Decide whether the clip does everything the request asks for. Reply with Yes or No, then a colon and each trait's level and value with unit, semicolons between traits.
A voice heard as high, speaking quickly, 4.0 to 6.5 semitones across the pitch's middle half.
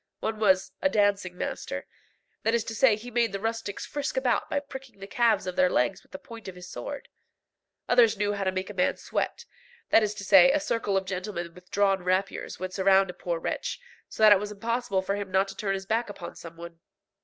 No: high, 205 Hz; fast, 235 wpm; average, 3.4 semitones